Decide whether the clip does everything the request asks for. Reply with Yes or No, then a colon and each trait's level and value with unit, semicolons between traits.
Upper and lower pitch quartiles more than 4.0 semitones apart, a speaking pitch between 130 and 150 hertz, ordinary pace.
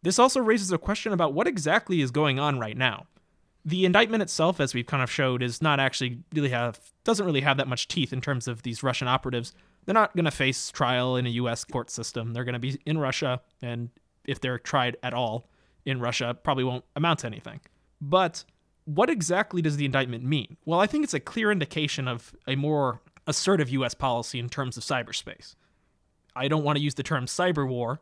No: average, 4.4 semitones; medium, 140 Hz; fast, 215 wpm